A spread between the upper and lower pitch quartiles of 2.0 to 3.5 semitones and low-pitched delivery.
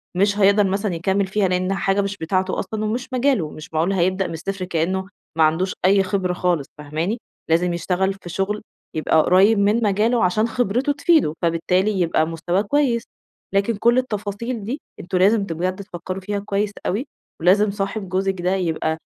No: average, 2.7 semitones; high, 195 Hz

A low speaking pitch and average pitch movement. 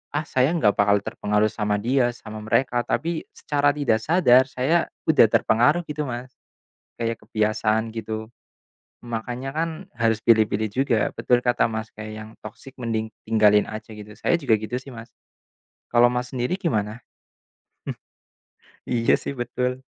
Yes: low, 115 Hz; average, 3.0 semitones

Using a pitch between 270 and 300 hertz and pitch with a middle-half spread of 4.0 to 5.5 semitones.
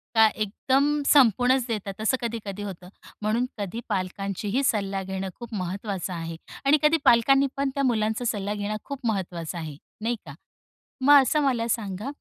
No: high, 215 Hz; average, 4.4 semitones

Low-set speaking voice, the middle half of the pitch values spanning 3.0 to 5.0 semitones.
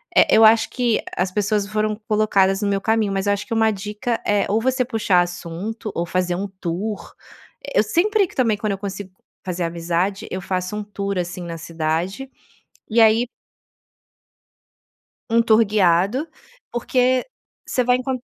No: high, 205 Hz; average, 3.5 semitones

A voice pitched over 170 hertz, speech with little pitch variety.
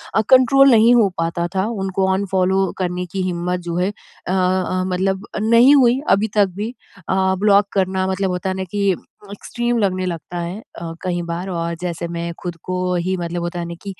Yes: high, 190 Hz; narrow, 2.3 semitones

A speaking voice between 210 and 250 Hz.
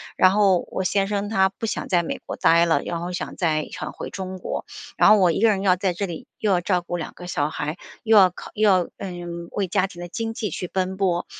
No: medium, 185 Hz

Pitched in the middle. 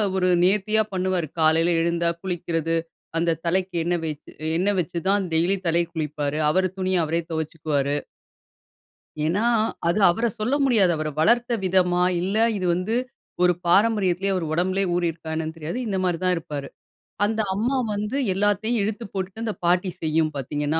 Yes: medium, 180 Hz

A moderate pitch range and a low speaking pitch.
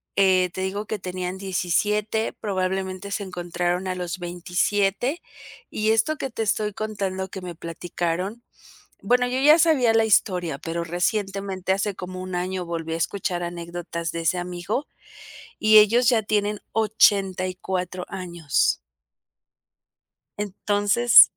No: average, 3.0 semitones; high, 190 Hz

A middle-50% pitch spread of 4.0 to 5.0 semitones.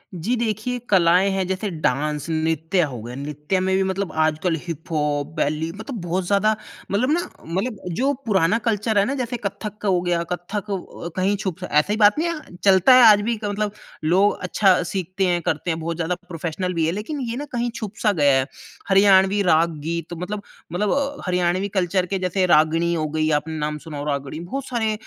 Yes: average, 4.3 semitones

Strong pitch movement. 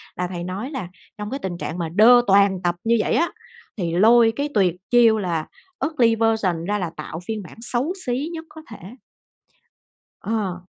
No: average, 5.0 semitones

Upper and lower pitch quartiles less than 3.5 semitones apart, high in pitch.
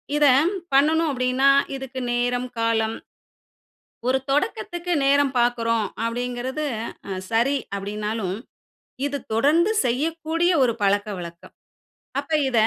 No: average, 4.2 semitones; very high, 255 Hz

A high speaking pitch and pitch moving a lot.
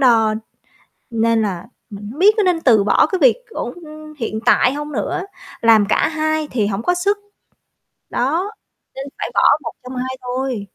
Yes: very high, 260 Hz; wide, 5.9 semitones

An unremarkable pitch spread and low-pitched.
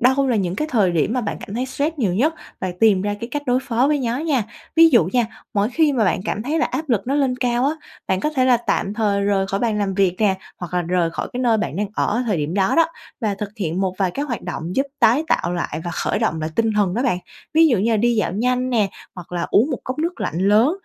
No: average, 5.0 semitones; high, 225 Hz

